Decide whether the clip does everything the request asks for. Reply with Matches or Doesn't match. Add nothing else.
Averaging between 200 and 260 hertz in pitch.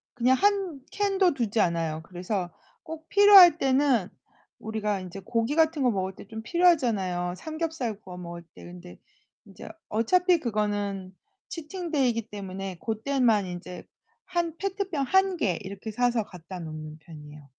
Matches